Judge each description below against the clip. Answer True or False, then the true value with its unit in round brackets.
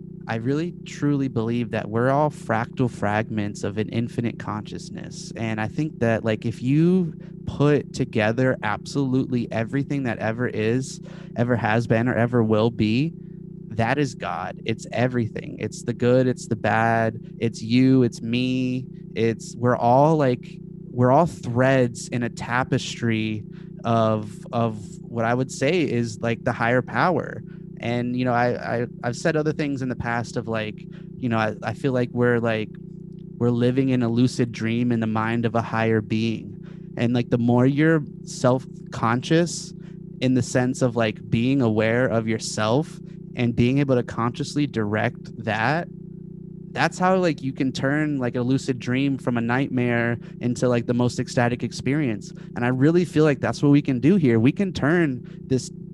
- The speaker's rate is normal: True (175 wpm)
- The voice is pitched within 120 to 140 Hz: True (125 Hz)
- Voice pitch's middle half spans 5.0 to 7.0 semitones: True (5.6 semitones)